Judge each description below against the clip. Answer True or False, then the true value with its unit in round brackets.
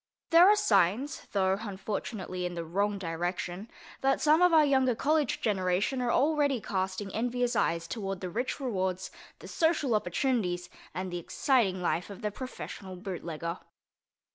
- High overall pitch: True (200 Hz)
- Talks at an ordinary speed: True (150 wpm)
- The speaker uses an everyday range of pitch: False (6.1 semitones)